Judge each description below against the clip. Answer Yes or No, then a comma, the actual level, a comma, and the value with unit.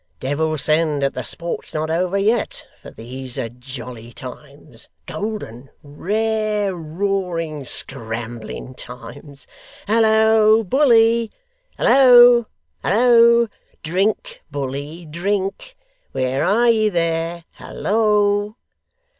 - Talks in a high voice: No, medium, 180 Hz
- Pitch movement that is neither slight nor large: No, wide, 7.5 semitones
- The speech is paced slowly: Yes, slow, 95 wpm